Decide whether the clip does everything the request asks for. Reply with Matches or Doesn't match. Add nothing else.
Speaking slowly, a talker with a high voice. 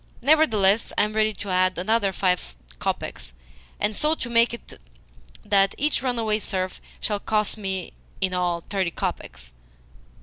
Doesn't match